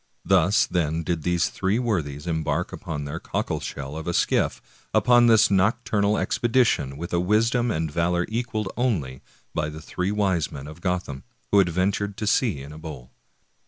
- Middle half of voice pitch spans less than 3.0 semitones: No, average, 5.3 semitones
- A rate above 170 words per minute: No, average, 165 wpm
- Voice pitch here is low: Yes, very low, 90 Hz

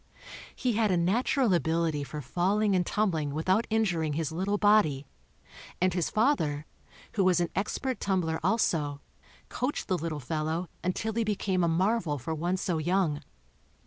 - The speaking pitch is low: No, medium, 180 Hz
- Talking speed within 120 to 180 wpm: Yes, average, 165 wpm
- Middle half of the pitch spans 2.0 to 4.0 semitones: No, average, 4.6 semitones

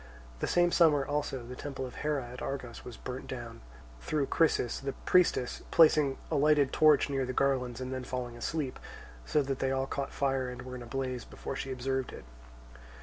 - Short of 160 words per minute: No, average, 200 wpm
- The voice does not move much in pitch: Yes, narrow, 2.1 semitones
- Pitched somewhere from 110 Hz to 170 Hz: Yes, low, 135 Hz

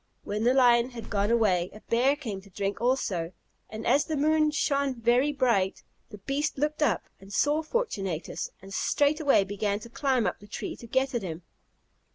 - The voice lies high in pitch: Yes, high, 235 Hz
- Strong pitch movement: Yes, wide, 5.8 semitones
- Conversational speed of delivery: Yes, average, 190 wpm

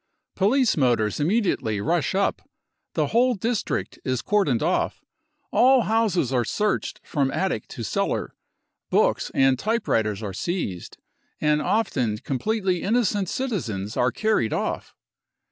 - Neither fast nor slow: No, slow, 130 wpm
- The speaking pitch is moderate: Yes, medium, 170 Hz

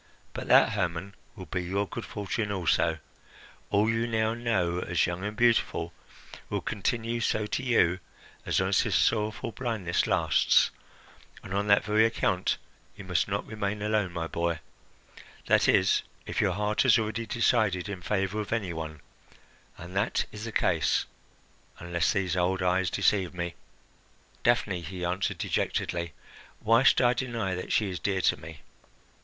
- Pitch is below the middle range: Yes, low, 100 Hz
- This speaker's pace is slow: No, average, 160 wpm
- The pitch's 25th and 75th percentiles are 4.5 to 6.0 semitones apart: No, average, 3.7 semitones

